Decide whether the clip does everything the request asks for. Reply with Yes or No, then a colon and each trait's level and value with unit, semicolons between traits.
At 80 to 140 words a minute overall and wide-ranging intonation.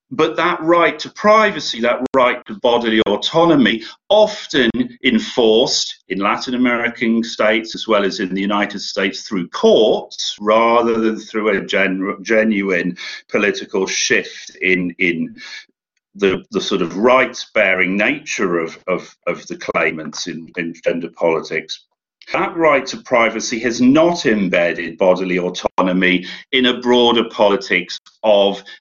Yes: slow, 135 wpm; wide, 9.0 semitones